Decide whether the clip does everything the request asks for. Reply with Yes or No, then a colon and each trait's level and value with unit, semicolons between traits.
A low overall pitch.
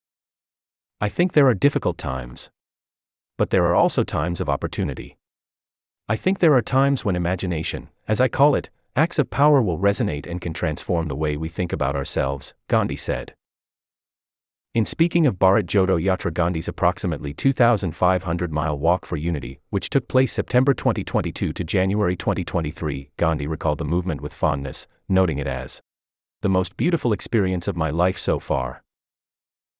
Yes: very low, 90 Hz